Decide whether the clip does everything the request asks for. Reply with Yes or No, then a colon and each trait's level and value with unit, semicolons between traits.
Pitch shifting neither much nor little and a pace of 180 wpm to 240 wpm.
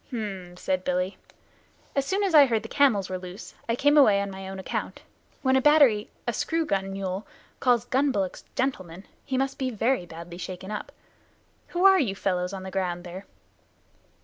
No: wide, 6.1 semitones; average, 190 wpm